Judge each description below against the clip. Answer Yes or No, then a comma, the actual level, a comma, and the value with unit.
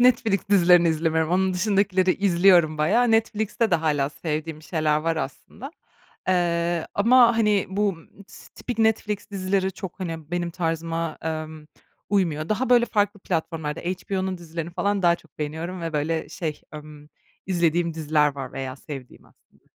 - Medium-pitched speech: Yes, medium, 170 Hz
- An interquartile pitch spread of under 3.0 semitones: No, average, 3.9 semitones